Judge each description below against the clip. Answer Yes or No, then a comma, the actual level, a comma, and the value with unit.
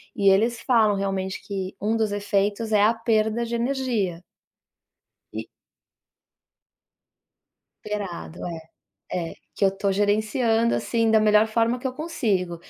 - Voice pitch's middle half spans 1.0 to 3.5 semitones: Yes, average, 2.7 semitones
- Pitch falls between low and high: No, high, 215 Hz